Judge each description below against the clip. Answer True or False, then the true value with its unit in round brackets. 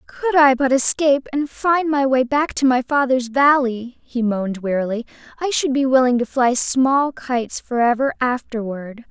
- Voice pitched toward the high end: True (260 Hz)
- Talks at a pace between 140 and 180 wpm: True (170 wpm)